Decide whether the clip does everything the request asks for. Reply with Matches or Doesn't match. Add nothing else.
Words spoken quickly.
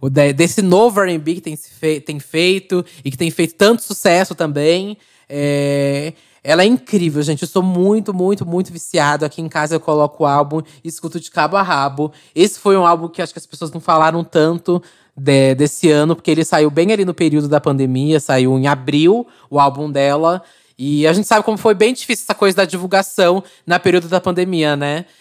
Matches